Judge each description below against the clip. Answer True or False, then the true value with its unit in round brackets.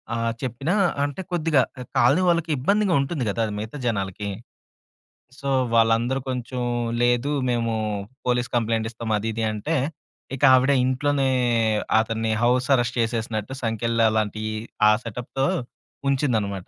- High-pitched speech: False (120 Hz)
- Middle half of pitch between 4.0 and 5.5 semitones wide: False (3.2 semitones)